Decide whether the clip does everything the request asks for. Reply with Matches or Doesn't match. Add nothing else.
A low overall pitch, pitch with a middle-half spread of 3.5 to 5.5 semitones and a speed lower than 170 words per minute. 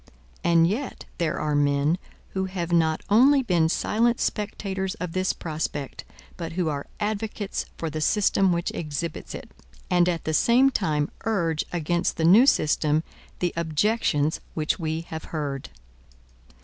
Doesn't match